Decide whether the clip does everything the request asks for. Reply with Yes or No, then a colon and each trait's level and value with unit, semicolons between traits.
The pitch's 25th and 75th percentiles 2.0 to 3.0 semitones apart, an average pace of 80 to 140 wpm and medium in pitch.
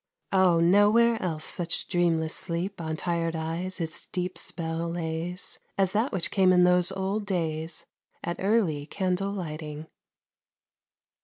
Yes: average, 2.7 semitones; slow, 135 wpm; medium, 175 Hz